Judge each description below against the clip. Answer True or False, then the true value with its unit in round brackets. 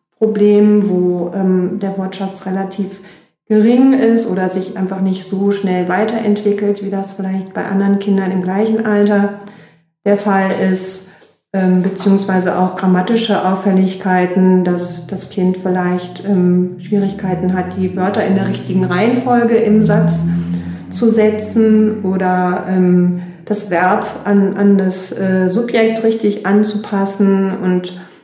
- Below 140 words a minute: True (130 wpm)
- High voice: True (195 Hz)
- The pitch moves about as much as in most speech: False (1.9 semitones)